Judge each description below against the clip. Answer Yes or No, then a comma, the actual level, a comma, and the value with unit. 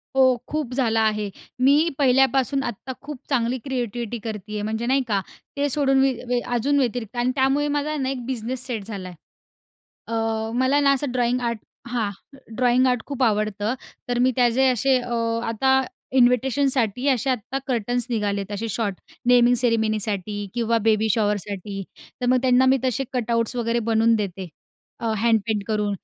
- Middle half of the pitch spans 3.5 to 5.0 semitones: No, average, 3.1 semitones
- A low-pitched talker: No, high, 240 Hz